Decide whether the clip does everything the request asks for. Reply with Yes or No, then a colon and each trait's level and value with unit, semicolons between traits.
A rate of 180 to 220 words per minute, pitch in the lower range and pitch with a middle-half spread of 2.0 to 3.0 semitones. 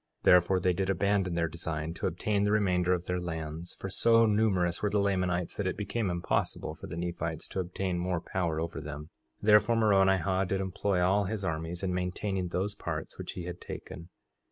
Yes: average, 200 wpm; very low, 90 Hz; narrow, 2.4 semitones